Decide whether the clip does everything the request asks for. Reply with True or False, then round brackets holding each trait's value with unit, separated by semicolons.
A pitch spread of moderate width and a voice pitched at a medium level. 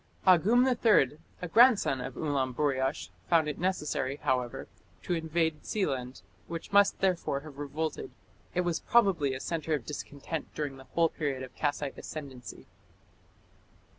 True (4.3 semitones; 150 Hz)